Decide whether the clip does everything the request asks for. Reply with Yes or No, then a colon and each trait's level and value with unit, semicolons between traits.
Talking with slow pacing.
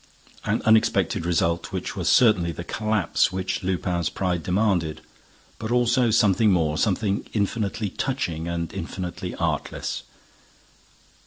Yes: slow, 115 wpm